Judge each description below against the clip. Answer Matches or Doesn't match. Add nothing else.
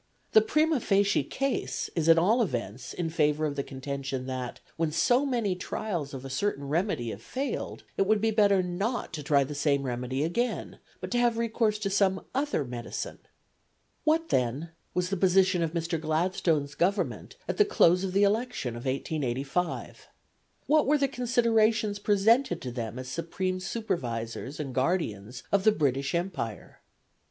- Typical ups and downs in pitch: Doesn't match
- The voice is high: Doesn't match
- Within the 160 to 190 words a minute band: Matches